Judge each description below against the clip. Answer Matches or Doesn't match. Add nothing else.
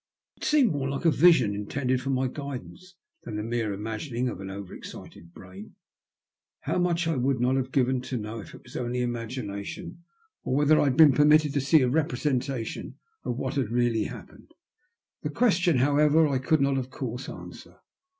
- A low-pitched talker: Matches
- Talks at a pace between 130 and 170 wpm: Doesn't match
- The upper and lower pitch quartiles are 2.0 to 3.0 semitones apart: Doesn't match